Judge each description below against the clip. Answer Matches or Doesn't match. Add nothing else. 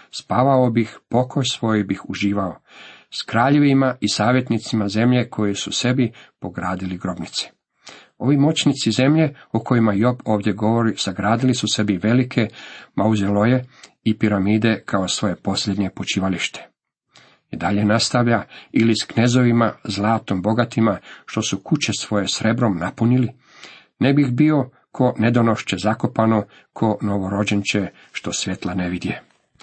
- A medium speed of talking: Matches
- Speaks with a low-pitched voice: Matches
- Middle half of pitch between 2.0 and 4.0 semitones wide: Matches